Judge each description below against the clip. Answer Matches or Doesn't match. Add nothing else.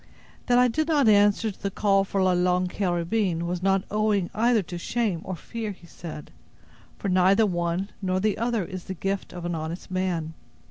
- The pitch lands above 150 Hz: Matches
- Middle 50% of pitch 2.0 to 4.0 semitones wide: Matches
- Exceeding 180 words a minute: Matches